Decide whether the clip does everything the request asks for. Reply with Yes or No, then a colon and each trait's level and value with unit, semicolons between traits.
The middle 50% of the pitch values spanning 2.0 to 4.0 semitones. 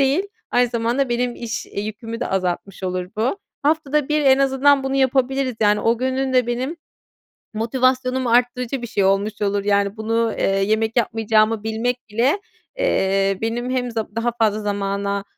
Yes: average, 3.7 semitones